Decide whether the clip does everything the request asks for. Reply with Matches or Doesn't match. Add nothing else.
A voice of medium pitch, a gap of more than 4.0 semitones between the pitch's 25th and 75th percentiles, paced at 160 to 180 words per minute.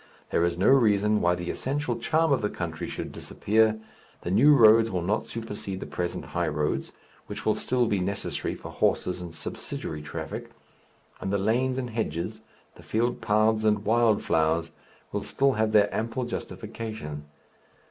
Doesn't match